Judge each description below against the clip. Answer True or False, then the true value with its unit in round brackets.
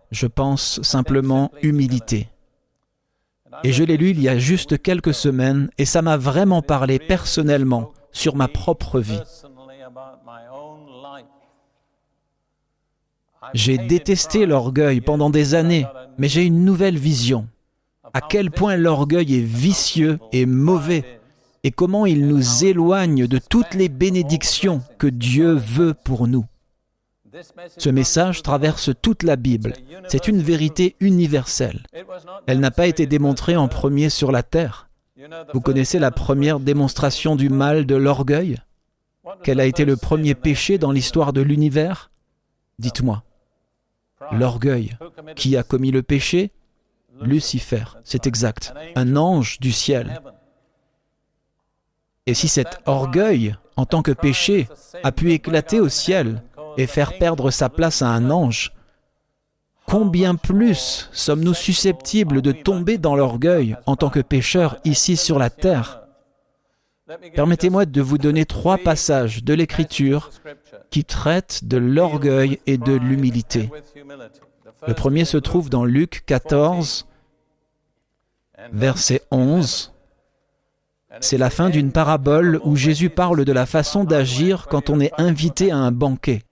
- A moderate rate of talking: False (130 wpm)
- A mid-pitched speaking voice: True (145 Hz)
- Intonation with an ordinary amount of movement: True (4.0 semitones)